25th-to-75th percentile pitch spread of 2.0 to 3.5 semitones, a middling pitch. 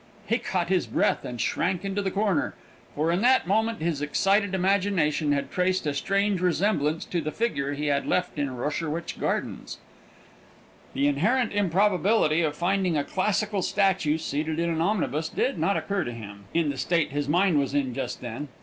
No: average, 5.1 semitones; medium, 170 Hz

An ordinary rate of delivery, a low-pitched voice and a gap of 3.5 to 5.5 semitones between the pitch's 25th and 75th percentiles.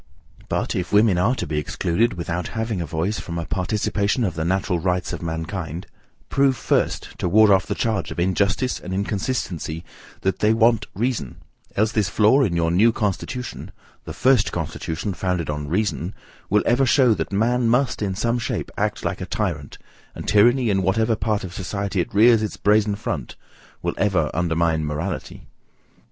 Yes: average, 175 wpm; low, 100 Hz; average, 4.4 semitones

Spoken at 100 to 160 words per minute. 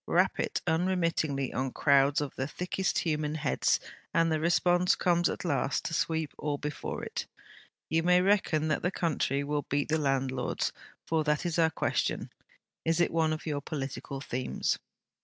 No: average, 175 wpm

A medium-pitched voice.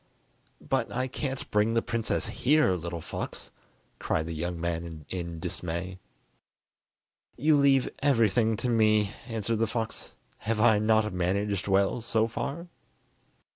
No: low, 110 Hz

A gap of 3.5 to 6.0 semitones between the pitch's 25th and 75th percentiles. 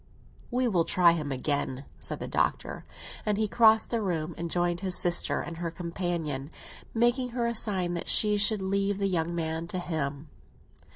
Yes: average, 4.2 semitones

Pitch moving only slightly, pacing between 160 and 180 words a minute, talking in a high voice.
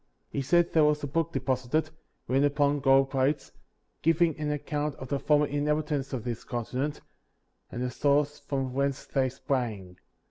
No: narrow, 2.2 semitones; average, 170 wpm; medium, 140 Hz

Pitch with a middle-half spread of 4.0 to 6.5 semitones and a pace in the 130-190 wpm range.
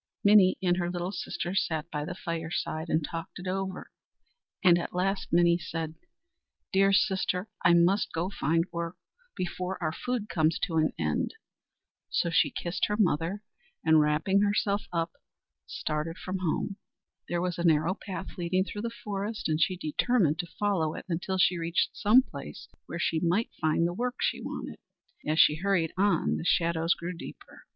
No: average, 2.8 semitones; average, 175 wpm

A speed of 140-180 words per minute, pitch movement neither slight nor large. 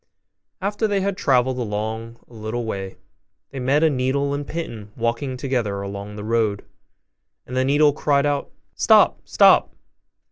Yes: average, 155 wpm; average, 4.6 semitones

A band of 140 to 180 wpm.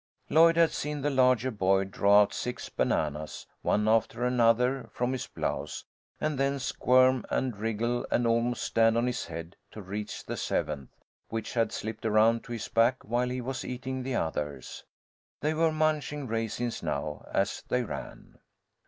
Yes: average, 165 wpm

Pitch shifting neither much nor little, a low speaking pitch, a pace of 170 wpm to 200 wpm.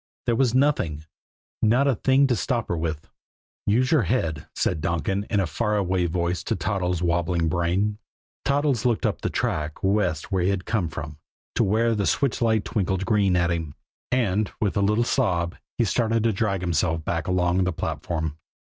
Yes: average, 4.8 semitones; very low, 95 Hz; average, 185 wpm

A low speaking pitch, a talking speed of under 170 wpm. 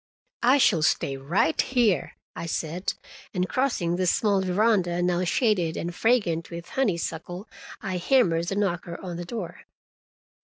No: medium, 180 Hz; average, 145 wpm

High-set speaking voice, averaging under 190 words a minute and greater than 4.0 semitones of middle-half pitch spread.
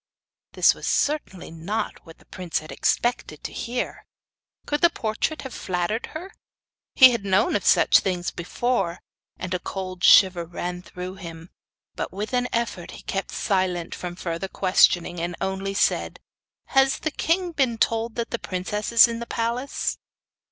Yes: high, 195 Hz; average, 165 wpm; average, 5.1 semitones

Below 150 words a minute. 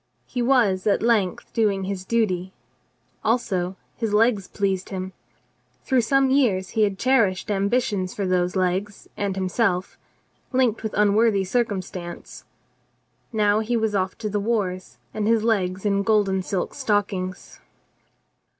Yes: average, 140 wpm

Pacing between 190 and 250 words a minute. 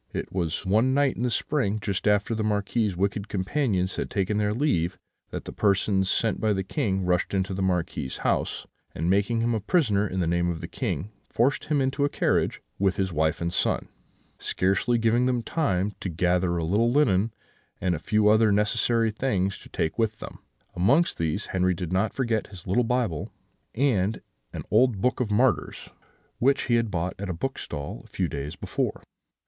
Yes: average, 195 wpm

